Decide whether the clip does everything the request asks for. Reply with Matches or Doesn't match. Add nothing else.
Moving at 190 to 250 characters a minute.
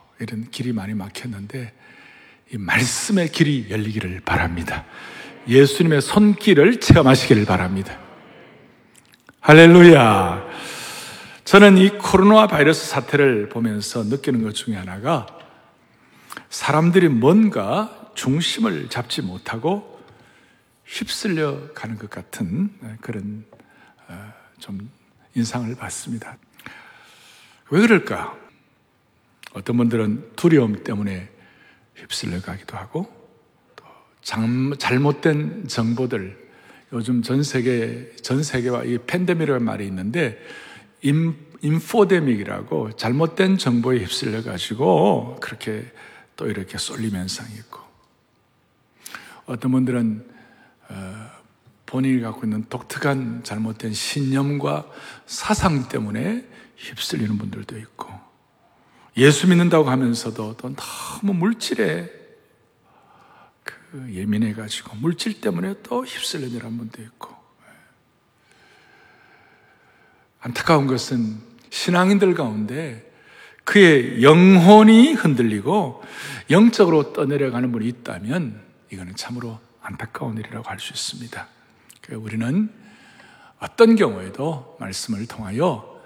Matches